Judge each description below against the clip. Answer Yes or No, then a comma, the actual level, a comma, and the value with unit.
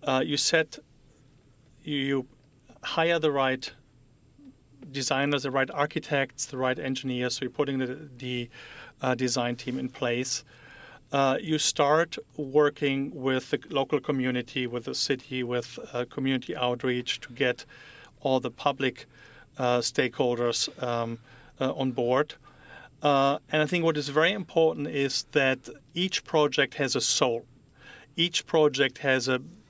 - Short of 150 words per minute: Yes, average, 140 wpm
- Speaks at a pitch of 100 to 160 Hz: Yes, low, 135 Hz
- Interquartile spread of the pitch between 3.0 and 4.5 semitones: No, narrow, 2.5 semitones